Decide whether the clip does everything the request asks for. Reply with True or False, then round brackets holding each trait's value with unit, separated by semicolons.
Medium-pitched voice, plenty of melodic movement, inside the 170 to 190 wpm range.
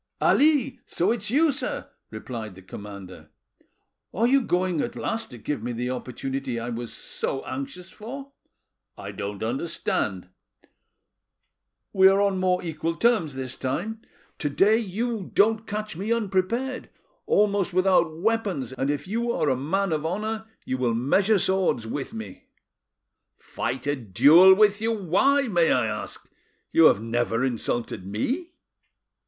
False (175 Hz; 9.0 semitones; 150 wpm)